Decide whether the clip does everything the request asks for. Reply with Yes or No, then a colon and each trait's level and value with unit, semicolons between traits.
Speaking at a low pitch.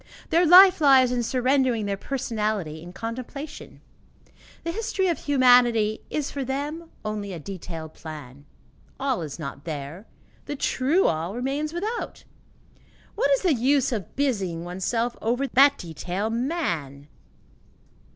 No: high, 240 Hz